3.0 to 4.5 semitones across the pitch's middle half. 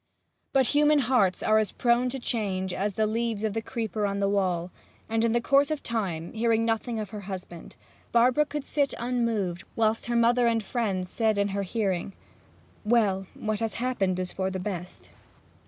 Yes: average, 3.5 semitones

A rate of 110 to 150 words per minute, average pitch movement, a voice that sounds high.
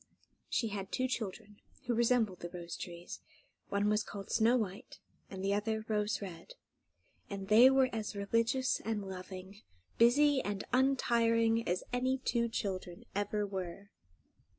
Yes: average, 145 wpm; average, 3.2 semitones; high, 210 Hz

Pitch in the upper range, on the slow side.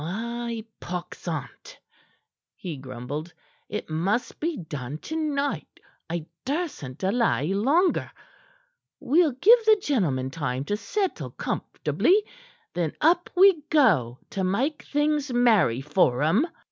Yes: high, 215 Hz; slow, 120 wpm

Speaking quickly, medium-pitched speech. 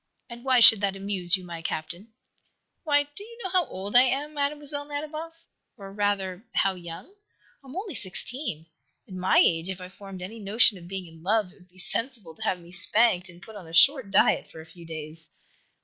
No: fast, 210 wpm; high, 195 Hz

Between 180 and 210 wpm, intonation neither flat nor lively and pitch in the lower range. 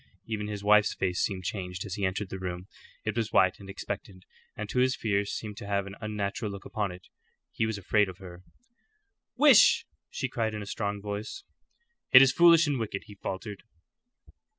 No: average, 195 wpm; narrow, 2.2 semitones; low, 105 Hz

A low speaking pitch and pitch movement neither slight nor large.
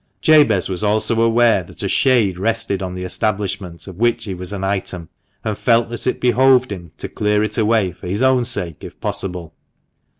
Yes: low, 105 Hz; average, 4.1 semitones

